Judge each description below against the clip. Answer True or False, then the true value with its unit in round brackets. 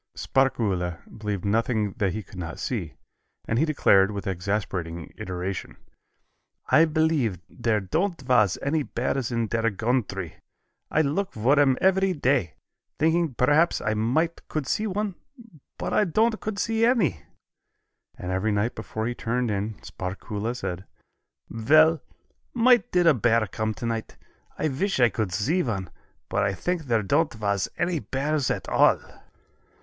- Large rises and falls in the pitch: True (7.5 semitones)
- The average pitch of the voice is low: True (120 Hz)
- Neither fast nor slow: True (150 wpm)